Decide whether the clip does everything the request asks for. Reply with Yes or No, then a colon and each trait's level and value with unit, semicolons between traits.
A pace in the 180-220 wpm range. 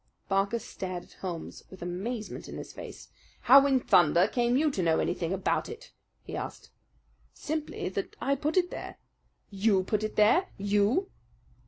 No: average, 165 wpm